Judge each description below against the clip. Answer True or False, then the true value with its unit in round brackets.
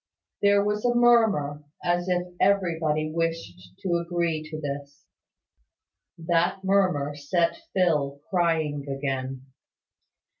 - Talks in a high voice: False (165 Hz)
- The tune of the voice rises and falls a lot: False (4.2 semitones)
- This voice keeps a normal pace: False (105 wpm)